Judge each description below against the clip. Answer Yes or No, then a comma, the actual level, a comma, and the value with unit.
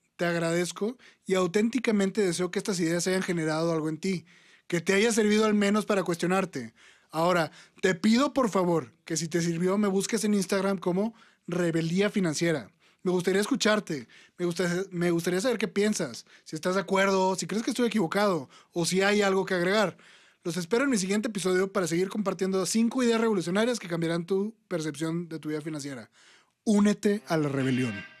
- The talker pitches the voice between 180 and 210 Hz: Yes, high, 190 Hz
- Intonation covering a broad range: No, average, 3.2 semitones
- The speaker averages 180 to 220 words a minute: Yes, average, 185 wpm